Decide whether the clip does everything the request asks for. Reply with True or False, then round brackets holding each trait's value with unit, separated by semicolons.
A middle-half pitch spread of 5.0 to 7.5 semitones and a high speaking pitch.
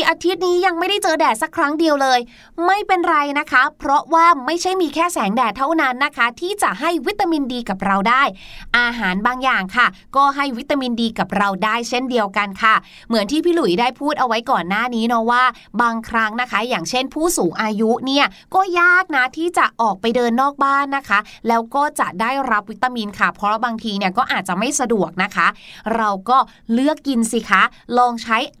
True (5.3 semitones; 250 Hz)